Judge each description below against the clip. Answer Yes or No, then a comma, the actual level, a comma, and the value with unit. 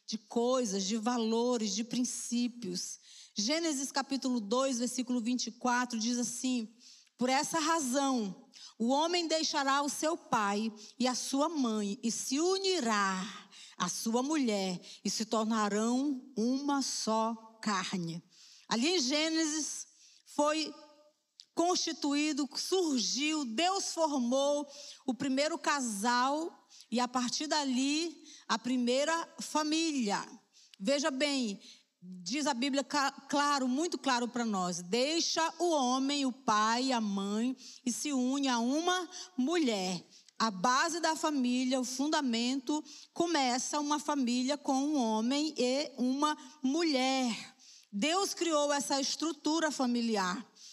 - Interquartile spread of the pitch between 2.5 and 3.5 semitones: No, average, 4.3 semitones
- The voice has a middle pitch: No, very high, 260 Hz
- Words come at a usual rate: No, slow, 115 wpm